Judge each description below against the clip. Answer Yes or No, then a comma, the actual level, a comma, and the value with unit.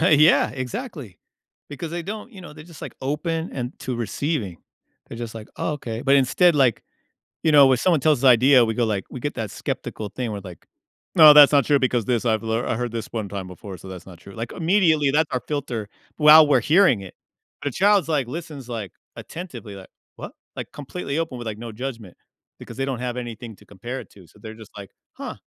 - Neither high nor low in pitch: No, low, 130 Hz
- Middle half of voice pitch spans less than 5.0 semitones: No, average, 5.3 semitones